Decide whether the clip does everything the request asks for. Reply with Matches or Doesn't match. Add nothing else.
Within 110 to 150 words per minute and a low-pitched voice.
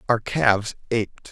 Matches